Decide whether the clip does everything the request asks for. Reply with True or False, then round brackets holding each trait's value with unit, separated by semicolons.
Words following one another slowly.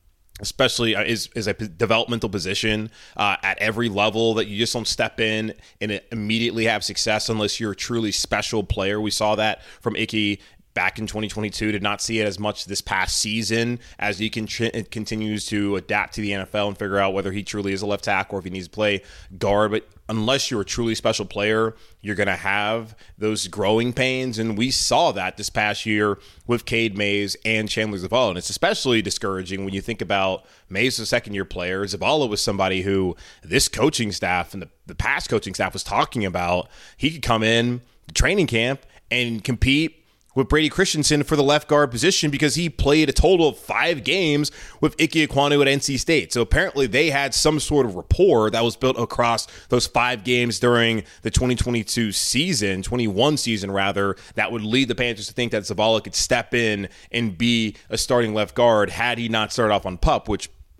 False (205 wpm)